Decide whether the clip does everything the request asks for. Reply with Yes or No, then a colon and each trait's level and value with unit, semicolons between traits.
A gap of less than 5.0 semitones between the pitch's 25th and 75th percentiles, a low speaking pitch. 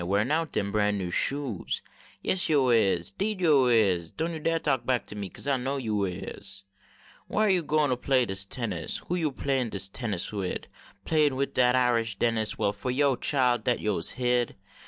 No: wide, 5.5 semitones; low, 125 Hz